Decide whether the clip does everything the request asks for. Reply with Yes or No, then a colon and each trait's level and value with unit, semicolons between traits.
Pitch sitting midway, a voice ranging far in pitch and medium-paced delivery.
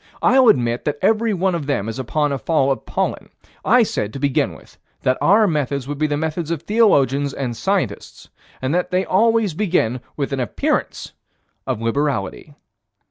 Yes: medium, 145 Hz; wide, 6.1 semitones; average, 175 wpm